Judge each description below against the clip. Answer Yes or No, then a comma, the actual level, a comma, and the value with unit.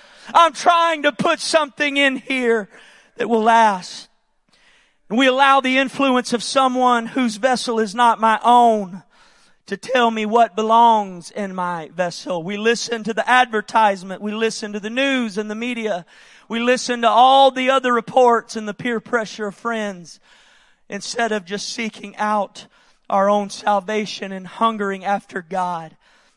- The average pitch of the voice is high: Yes, high, 225 Hz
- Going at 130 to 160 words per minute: Yes, average, 155 wpm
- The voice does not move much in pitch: No, average, 3.4 semitones